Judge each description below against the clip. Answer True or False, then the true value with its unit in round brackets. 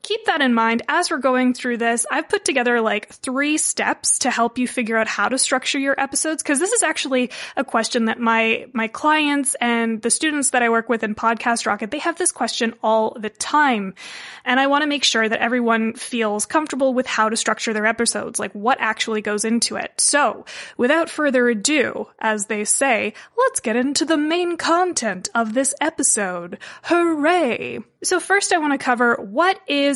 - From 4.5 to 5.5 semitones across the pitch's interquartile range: True (4.9 semitones)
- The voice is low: False (250 Hz)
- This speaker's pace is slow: False (200 wpm)